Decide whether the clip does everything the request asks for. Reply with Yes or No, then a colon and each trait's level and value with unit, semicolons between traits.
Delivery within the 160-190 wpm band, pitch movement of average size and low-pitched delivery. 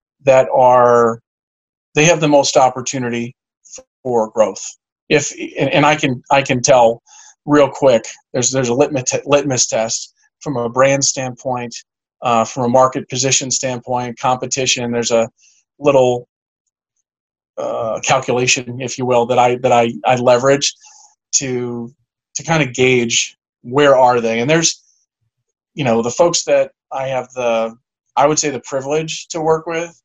No: average, 150 wpm; average, 3.1 semitones; low, 130 Hz